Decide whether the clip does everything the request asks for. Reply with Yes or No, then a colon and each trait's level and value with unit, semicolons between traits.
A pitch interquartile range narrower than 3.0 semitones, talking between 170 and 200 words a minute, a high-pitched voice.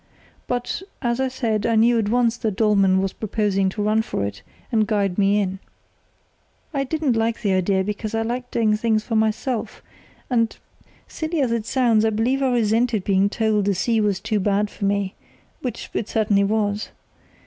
Yes: narrow, 2.6 semitones; average, 185 wpm; high, 220 Hz